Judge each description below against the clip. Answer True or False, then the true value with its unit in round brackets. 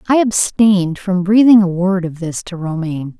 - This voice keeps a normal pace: True (190 wpm)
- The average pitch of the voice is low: False (185 Hz)